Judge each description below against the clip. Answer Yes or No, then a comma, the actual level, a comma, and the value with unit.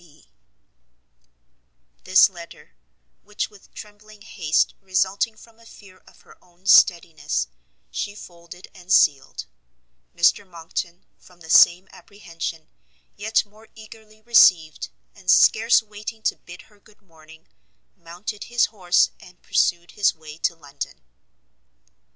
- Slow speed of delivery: Yes, slow, 125 wpm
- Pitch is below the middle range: No, medium, 185 Hz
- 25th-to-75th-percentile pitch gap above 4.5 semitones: No, average, 3.8 semitones